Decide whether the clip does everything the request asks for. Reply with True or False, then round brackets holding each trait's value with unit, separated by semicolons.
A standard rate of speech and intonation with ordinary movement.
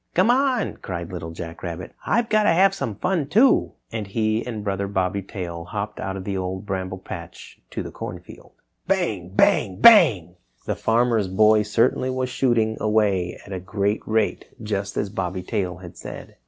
True (180 wpm; 4.4 semitones)